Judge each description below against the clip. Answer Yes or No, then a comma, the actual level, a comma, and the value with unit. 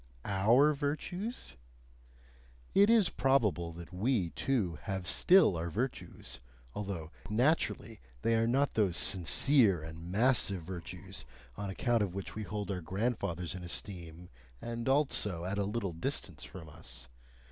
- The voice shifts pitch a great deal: Yes, wide, 6.0 semitones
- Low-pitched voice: Yes, low, 100 Hz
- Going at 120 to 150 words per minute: Yes, slow, 135 wpm